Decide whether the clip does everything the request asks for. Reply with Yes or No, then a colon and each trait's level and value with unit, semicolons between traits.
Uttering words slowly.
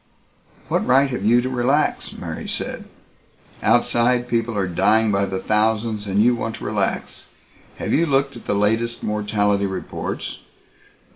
No: average, 150 wpm